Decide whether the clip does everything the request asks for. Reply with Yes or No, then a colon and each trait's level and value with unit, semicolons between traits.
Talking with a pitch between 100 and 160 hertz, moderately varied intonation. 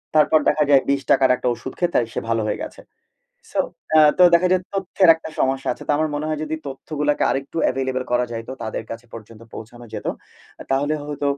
Yes: medium, 140 Hz; average, 3.8 semitones